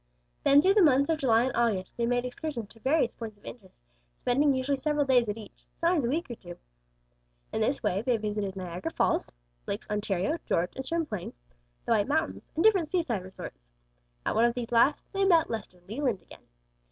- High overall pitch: Yes, high, 245 Hz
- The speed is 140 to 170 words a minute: No, average, 200 wpm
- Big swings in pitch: Yes, wide, 6.0 semitones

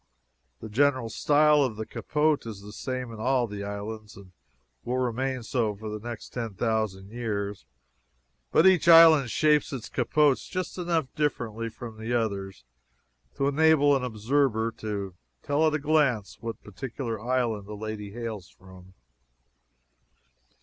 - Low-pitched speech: Yes, low, 115 Hz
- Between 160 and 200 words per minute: No, average, 150 wpm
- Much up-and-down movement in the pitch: No, average, 4.9 semitones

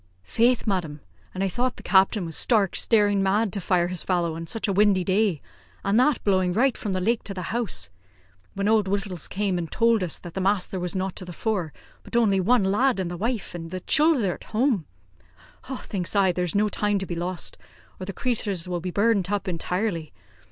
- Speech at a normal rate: No, fast, 215 wpm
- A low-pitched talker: No, high, 195 Hz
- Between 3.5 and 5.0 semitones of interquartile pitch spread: No, average, 3.1 semitones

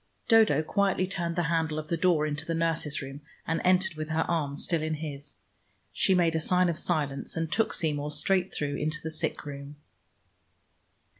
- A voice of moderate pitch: Yes, medium, 160 Hz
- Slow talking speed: No, average, 190 wpm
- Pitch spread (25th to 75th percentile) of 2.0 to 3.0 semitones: Yes, narrow, 2.5 semitones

